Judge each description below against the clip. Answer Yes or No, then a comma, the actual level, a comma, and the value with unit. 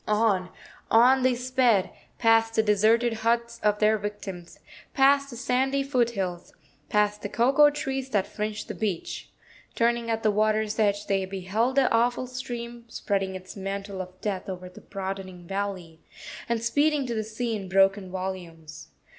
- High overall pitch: Yes, high, 215 Hz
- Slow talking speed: No, average, 155 wpm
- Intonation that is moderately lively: Yes, average, 3.6 semitones